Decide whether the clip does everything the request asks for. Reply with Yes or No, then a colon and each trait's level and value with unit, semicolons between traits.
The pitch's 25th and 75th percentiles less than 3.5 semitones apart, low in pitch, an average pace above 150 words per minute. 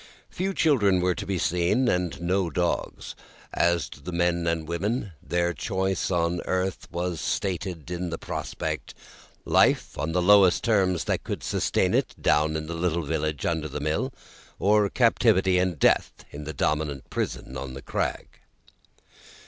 Yes: average, 2.8 semitones; very low, 85 Hz; average, 160 wpm